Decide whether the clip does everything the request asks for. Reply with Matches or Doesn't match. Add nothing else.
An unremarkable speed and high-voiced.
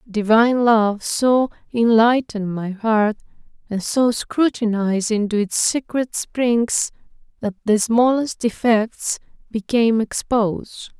Doesn't match